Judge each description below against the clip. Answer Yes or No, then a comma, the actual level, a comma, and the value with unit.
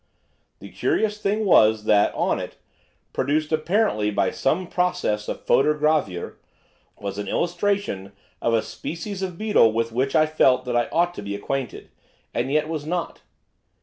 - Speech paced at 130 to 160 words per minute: Yes, average, 155 wpm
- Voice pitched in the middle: Yes, medium, 150 Hz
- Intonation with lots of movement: Yes, wide, 7.9 semitones